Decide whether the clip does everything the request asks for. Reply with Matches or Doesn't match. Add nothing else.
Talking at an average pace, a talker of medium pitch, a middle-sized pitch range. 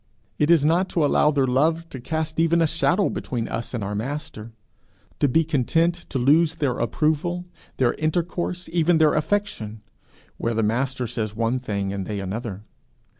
Doesn't match